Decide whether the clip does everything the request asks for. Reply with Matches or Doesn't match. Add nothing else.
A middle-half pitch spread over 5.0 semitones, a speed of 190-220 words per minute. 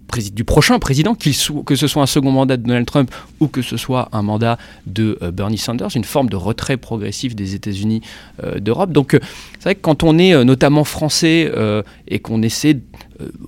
Matches